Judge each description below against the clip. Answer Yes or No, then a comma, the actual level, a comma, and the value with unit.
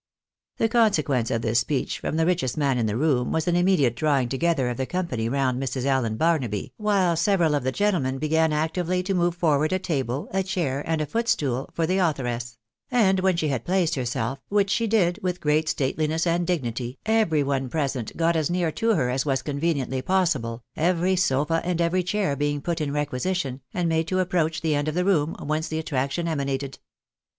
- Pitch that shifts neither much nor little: Yes, average, 4.9 semitones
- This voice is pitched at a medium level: Yes, medium, 155 Hz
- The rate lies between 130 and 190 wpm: No, fast, 205 wpm